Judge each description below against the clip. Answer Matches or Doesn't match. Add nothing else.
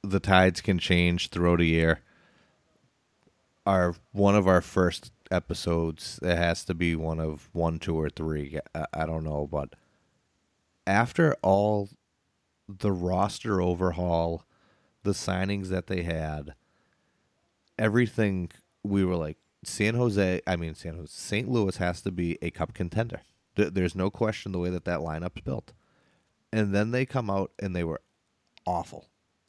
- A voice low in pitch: Matches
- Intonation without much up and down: Doesn't match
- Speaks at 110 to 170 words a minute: Matches